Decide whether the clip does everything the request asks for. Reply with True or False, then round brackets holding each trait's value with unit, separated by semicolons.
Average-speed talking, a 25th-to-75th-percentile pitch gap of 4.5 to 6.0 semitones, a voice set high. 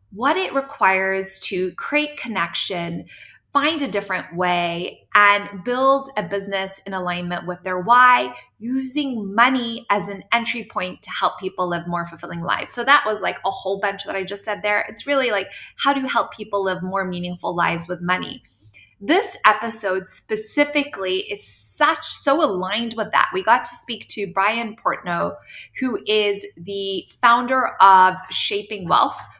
True (165 wpm; 4.9 semitones; 200 Hz)